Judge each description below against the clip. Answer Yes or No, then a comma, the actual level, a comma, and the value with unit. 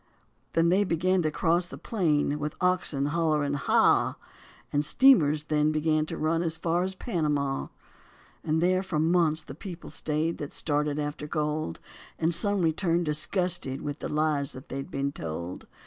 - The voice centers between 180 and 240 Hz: No, medium, 155 Hz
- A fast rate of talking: No, average, 165 wpm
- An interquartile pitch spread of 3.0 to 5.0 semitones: No, narrow, 2.6 semitones